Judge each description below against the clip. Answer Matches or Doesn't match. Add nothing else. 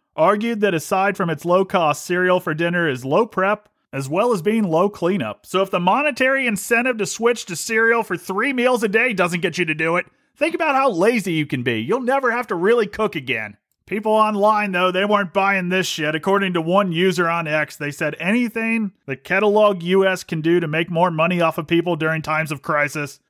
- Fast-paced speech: Matches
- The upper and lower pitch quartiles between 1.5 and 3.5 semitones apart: Doesn't match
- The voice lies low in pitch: Doesn't match